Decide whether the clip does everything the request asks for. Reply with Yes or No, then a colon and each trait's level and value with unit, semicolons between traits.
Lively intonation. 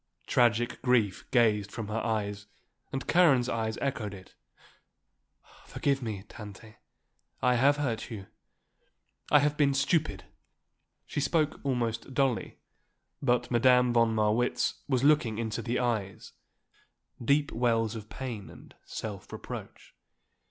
No: average, 3.5 semitones